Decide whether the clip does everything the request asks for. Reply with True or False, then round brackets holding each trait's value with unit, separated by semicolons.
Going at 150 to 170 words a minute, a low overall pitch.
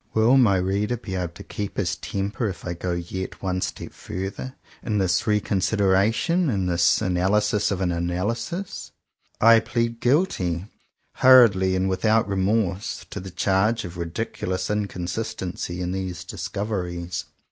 True (160 wpm; 95 Hz)